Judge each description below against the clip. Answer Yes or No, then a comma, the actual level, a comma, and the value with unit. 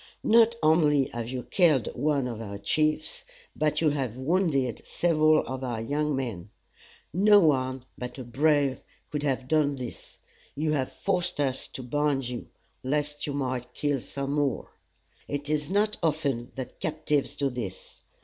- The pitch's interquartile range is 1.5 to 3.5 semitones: Yes, average, 3.2 semitones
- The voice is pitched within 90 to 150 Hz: Yes, medium, 140 Hz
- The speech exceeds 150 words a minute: Yes, average, 160 wpm